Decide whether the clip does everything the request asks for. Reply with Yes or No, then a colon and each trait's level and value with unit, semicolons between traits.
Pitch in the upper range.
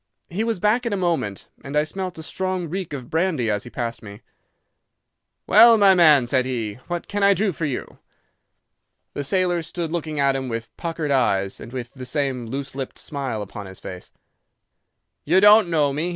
No: medium, 150 Hz